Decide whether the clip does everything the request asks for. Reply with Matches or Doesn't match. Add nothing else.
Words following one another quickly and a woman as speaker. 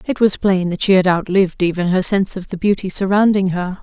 Matches